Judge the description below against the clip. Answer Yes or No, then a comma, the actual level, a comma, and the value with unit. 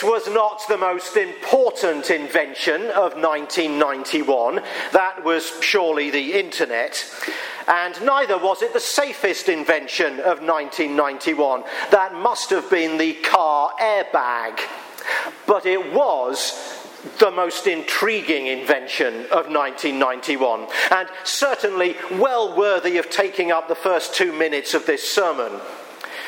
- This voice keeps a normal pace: No, slow, 120 wpm